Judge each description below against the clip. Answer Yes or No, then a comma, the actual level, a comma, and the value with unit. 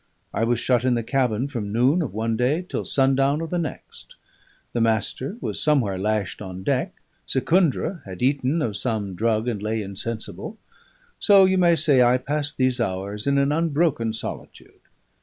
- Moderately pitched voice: No, low, 125 Hz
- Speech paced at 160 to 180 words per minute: Yes, average, 175 wpm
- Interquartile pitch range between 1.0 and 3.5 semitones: No, average, 5.1 semitones